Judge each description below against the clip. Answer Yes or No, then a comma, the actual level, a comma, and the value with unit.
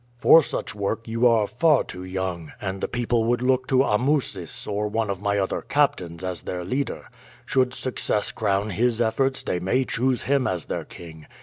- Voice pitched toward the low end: Yes, low, 110 Hz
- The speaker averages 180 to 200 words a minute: Yes, average, 190 wpm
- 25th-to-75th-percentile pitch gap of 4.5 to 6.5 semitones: Yes, average, 5.2 semitones